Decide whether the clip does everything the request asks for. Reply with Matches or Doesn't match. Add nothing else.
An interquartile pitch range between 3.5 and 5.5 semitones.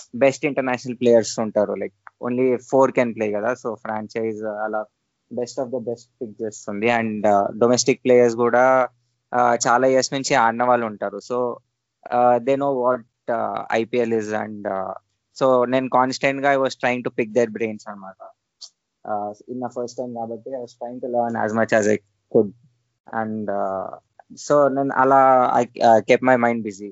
Doesn't match